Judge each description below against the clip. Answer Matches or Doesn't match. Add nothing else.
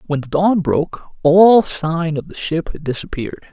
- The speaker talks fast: Doesn't match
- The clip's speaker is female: Doesn't match